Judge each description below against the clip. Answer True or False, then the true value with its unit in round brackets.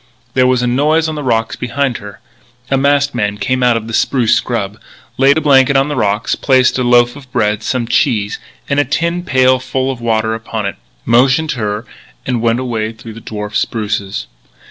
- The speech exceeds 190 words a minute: True (200 wpm)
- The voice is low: True (125 Hz)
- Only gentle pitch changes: False (3.3 semitones)